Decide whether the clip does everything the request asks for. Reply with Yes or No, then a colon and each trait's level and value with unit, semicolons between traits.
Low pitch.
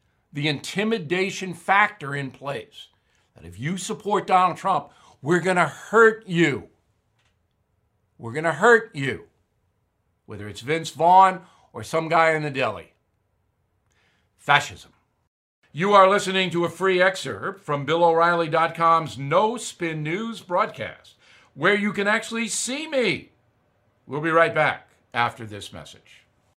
No: medium, 165 Hz